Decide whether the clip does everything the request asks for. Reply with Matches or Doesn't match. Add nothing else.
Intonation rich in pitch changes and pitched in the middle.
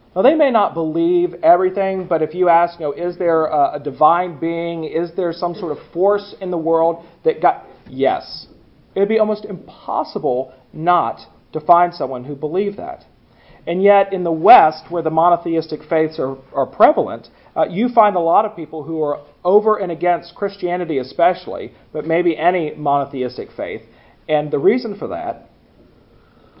Doesn't match